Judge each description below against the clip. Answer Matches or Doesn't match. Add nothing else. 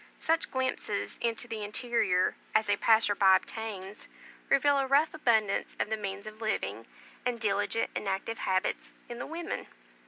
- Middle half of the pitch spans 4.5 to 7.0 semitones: Doesn't match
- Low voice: Doesn't match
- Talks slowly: Doesn't match